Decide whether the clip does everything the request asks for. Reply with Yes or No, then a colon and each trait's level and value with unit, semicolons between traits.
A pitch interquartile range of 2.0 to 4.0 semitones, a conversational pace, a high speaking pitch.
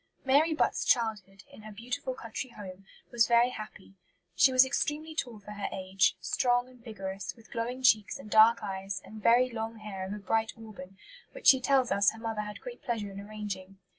Yes: average, 3.7 semitones; average, 195 wpm; high, 220 Hz